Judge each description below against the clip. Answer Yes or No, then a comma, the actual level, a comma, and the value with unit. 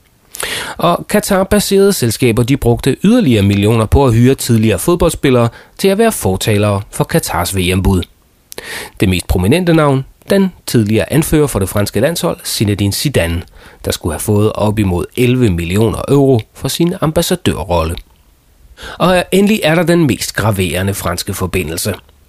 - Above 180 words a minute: No, slow, 145 wpm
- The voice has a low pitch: Yes, low, 115 Hz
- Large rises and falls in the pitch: Yes, wide, 8.9 semitones